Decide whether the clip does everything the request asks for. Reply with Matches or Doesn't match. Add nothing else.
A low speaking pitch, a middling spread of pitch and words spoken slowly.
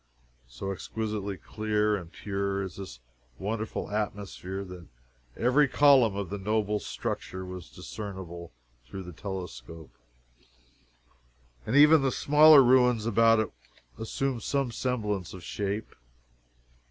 Matches